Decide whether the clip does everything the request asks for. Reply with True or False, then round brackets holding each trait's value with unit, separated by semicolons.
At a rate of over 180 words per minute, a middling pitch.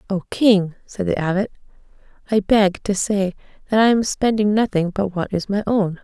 False (190 wpm; 200 Hz)